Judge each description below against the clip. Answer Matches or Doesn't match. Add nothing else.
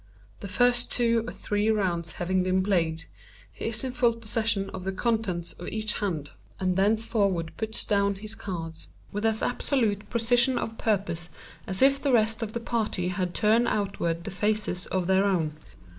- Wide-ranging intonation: Doesn't match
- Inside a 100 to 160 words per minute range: Doesn't match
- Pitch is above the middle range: Matches